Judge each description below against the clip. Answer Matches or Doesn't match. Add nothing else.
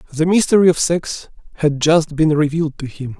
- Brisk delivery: Doesn't match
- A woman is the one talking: Doesn't match